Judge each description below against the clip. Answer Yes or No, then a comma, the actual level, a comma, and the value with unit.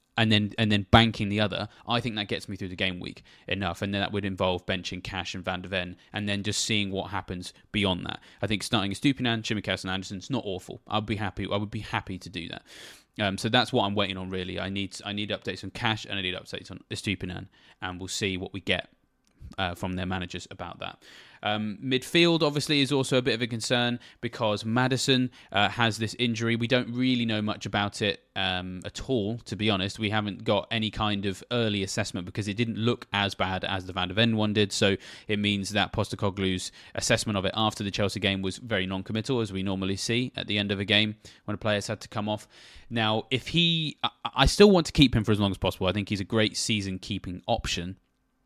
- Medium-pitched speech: No, low, 105 Hz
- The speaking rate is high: Yes, fast, 245 wpm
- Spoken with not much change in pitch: No, average, 3.0 semitones